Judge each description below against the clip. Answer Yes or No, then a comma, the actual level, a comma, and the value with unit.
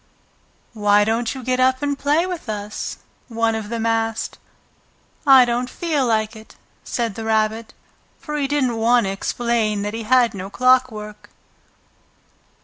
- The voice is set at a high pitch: Yes, high, 230 Hz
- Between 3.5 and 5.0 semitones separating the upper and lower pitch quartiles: No, average, 3.0 semitones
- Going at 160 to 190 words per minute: No, average, 150 wpm